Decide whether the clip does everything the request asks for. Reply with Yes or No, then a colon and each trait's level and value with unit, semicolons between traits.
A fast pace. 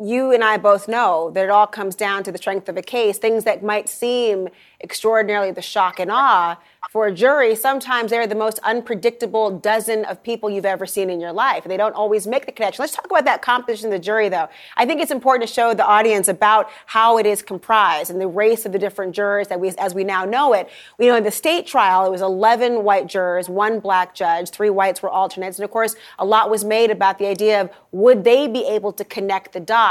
Yes: fast, 245 wpm